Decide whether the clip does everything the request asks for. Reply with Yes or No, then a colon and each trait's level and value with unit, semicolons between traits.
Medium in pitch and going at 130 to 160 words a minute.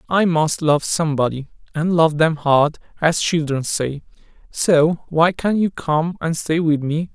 No: medium, 160 Hz; average, 170 wpm